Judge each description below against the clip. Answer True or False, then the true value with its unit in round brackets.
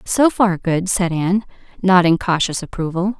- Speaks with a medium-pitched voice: True (180 Hz)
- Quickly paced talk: False (150 wpm)